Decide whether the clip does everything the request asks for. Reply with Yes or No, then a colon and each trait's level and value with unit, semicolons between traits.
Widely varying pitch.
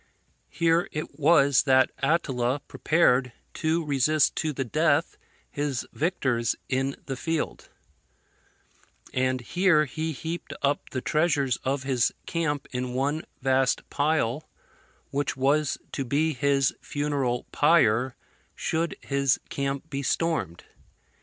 No: average, 3.1 semitones